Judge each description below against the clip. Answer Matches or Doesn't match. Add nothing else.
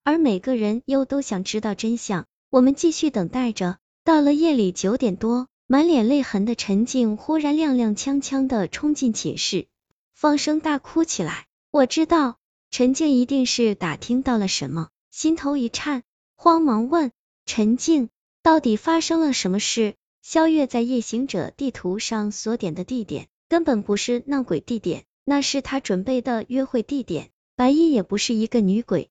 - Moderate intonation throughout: Matches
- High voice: Matches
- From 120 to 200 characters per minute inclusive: Doesn't match